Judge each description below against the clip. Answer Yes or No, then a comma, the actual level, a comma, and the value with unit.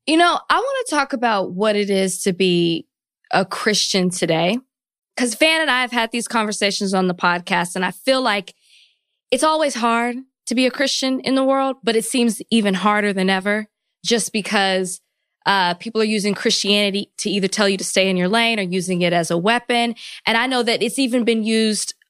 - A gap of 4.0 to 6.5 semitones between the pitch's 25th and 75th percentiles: Yes, average, 4.4 semitones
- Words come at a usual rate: No, fast, 210 wpm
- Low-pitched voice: No, high, 220 Hz